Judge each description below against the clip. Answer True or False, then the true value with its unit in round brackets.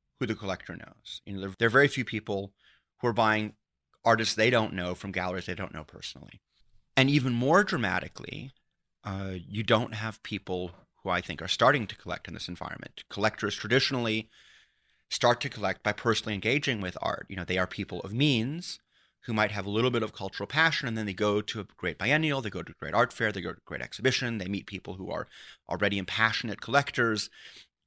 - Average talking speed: False (210 wpm)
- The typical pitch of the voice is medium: False (110 Hz)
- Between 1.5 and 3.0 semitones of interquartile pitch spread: False (3.8 semitones)